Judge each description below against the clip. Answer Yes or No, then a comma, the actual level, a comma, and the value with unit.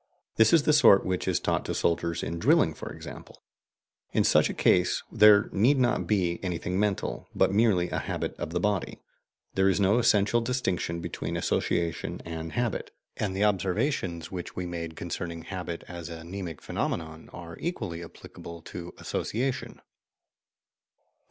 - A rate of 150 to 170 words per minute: Yes, average, 160 wpm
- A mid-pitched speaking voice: No, very low, 90 Hz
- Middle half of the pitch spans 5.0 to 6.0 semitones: No, average, 3.8 semitones